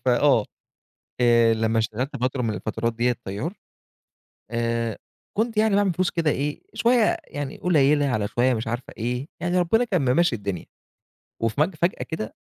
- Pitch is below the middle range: Yes, low, 130 Hz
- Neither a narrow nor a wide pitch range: No, wide, 7.0 semitones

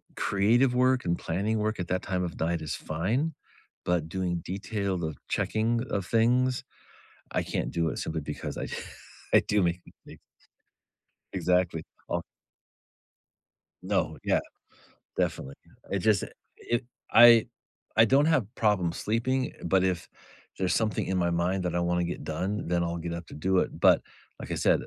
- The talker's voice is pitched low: Yes, very low, 95 Hz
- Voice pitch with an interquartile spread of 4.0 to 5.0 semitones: Yes, average, 4.4 semitones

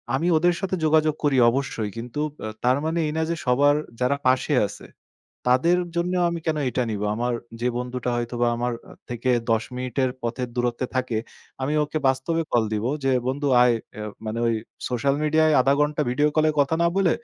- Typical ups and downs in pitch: Yes, average, 3.9 semitones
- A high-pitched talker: No, low, 130 Hz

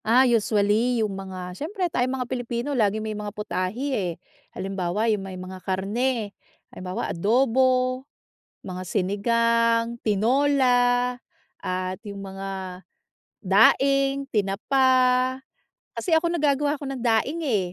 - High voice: Yes, high, 230 Hz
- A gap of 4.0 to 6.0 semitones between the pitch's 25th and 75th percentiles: Yes, average, 4.8 semitones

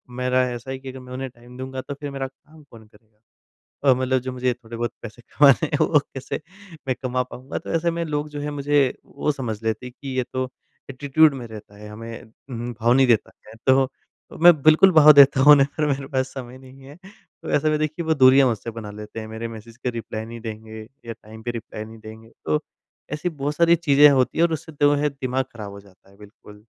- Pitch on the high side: No, low, 130 Hz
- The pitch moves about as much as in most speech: Yes, average, 3.9 semitones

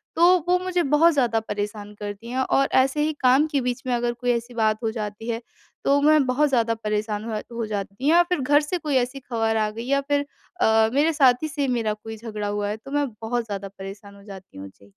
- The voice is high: Yes, high, 235 Hz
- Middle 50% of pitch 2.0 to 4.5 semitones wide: No, average, 4.9 semitones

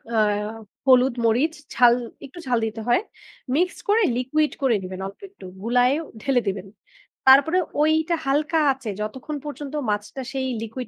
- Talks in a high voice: Yes, very high, 260 Hz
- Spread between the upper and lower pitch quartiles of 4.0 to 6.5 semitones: Yes, average, 4.5 semitones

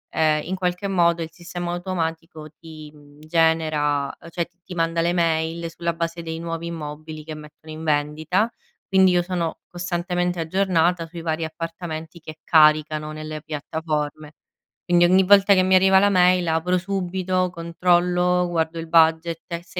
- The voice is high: No, medium, 165 Hz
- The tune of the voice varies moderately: No, narrow, 2.0 semitones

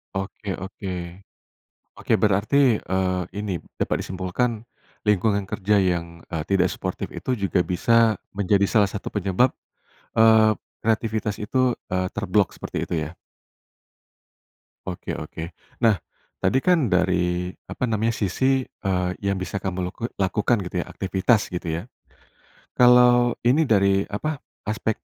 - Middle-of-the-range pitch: No, low, 100 Hz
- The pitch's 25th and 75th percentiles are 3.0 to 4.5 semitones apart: Yes, average, 3.5 semitones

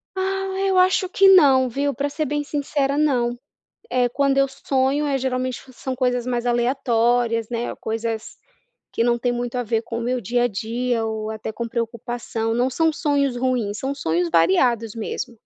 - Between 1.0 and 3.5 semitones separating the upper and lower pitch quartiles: Yes, average, 3.0 semitones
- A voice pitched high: Yes, high, 245 Hz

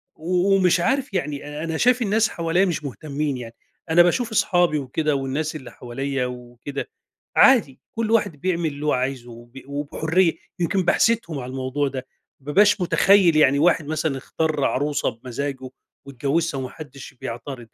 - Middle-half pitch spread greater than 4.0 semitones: Yes, average, 4.7 semitones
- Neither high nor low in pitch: Yes, medium, 150 Hz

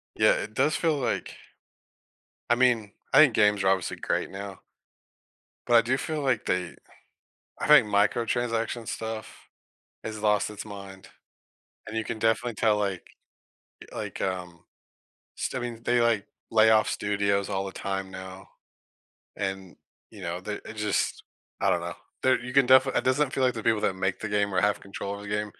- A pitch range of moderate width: Yes, average, 3.4 semitones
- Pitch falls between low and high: No, low, 105 Hz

